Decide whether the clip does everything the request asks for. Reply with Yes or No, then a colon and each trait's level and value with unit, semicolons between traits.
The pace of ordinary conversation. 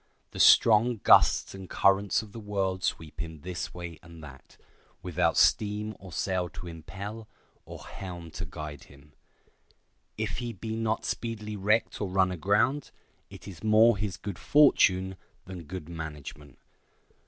Yes: average, 150 wpm